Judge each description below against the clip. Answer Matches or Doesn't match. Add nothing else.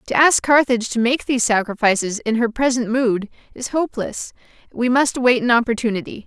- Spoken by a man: Doesn't match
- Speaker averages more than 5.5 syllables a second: Matches